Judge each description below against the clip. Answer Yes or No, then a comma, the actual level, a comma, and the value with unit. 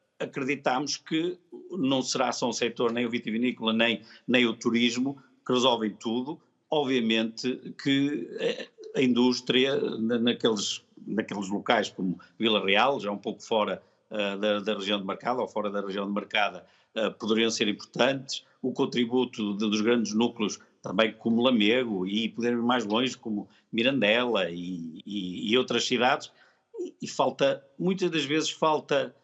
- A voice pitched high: No, low, 120 Hz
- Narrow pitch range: No, average, 4.2 semitones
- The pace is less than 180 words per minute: Yes, average, 150 wpm